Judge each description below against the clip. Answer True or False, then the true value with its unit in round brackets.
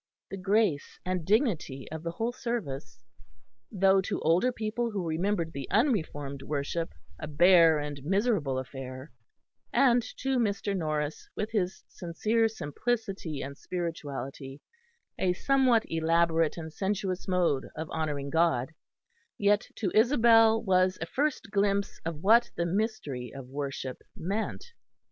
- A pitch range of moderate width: False (6.3 semitones)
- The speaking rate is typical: False (130 wpm)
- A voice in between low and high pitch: True (180 Hz)